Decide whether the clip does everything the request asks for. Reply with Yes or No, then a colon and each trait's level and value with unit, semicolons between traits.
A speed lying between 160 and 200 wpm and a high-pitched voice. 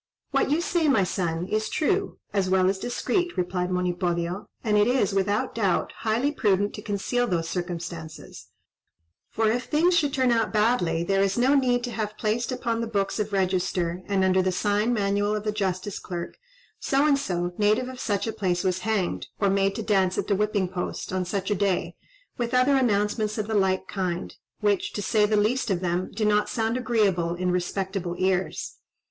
Yes: average, 195 wpm; high, 205 Hz